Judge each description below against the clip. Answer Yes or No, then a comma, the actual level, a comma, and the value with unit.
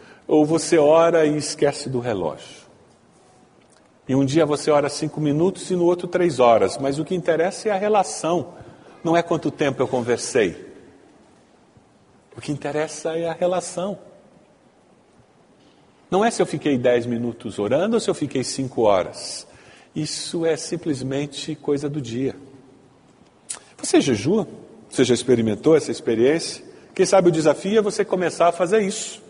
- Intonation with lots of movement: No, average, 4.9 semitones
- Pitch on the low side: No, medium, 155 Hz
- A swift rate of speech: No, average, 155 wpm